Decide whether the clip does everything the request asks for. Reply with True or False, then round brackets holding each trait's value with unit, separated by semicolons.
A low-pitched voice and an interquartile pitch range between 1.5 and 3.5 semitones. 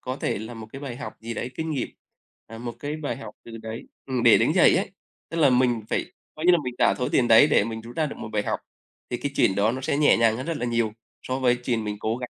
True (120 Hz; 3.1 semitones)